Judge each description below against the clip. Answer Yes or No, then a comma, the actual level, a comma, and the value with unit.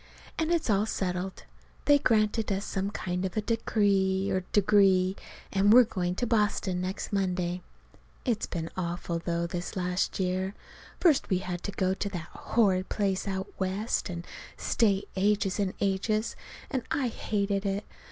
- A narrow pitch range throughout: Yes, narrow, 2.3 semitones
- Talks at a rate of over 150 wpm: Yes, average, 160 wpm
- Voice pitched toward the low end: No, high, 195 Hz